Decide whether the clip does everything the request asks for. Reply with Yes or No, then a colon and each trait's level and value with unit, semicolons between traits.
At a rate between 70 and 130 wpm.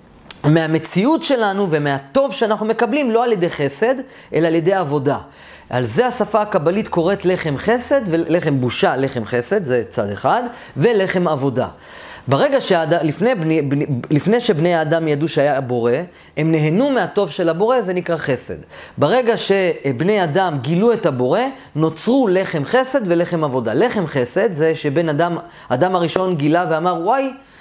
No: average, 145 wpm